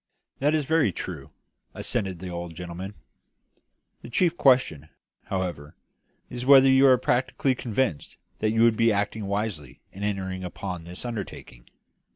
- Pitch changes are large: Yes, wide, 5.9 semitones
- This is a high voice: No, low, 105 Hz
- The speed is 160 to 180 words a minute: No, average, 145 wpm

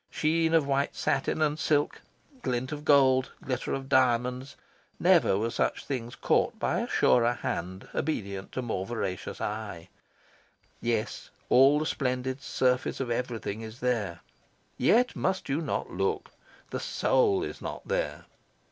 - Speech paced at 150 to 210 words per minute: No, average, 140 wpm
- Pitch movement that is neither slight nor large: Yes, average, 3.9 semitones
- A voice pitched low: Yes, low, 130 Hz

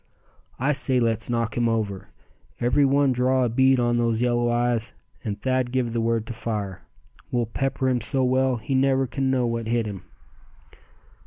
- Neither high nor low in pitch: No, low, 120 Hz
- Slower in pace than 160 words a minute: No, average, 180 wpm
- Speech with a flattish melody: Yes, narrow, 2.3 semitones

